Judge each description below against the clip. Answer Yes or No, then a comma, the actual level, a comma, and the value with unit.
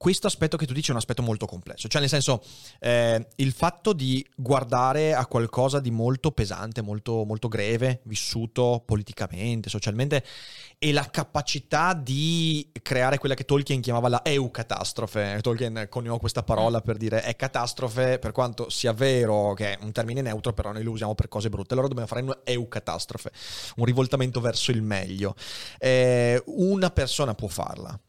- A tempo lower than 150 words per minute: No, fast, 170 wpm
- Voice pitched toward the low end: Yes, low, 120 Hz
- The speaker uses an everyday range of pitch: Yes, average, 3.4 semitones